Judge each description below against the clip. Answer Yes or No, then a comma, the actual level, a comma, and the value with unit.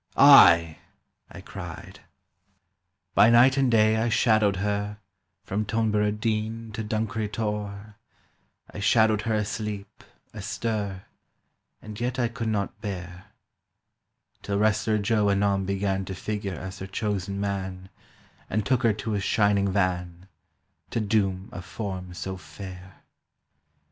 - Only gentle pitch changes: Yes, narrow, 2.2 semitones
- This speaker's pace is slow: Yes, slow, 130 wpm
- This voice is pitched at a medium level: No, low, 105 Hz